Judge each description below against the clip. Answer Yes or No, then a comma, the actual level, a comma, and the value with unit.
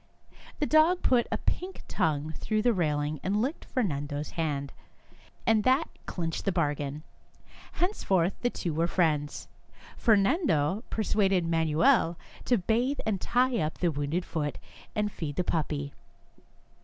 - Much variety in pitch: Yes, wide, 7.2 semitones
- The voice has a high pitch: No, medium, 180 Hz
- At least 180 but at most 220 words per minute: No, average, 140 wpm